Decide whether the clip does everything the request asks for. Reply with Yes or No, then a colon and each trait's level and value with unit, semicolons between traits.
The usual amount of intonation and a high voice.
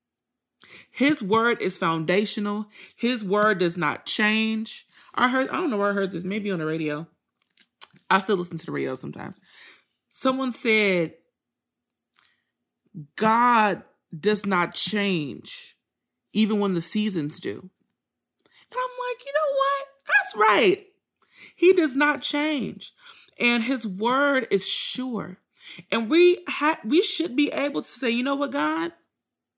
No: wide, 6.6 semitones; high, 225 Hz